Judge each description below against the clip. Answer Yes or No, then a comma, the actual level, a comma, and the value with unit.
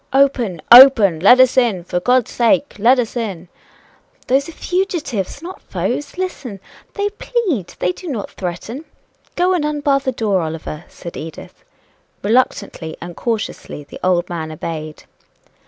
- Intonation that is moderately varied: No, wide, 7.9 semitones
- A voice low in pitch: No, high, 235 Hz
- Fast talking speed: No, average, 145 wpm